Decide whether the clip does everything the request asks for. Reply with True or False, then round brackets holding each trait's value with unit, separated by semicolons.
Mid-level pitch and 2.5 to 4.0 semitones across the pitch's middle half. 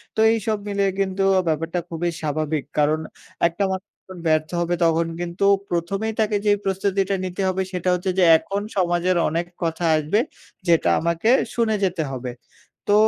True (175 Hz; 3.2 semitones)